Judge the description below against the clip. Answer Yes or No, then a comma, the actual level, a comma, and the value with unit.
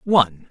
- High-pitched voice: No, low, 135 Hz